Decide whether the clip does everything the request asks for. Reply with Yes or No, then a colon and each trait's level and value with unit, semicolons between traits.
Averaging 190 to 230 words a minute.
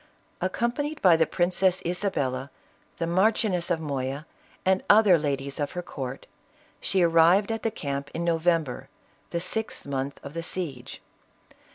No: average, 150 wpm